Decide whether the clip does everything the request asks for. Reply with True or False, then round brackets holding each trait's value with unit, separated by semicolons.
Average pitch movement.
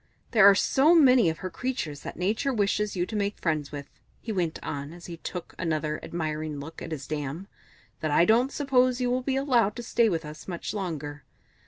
False (7.5 semitones)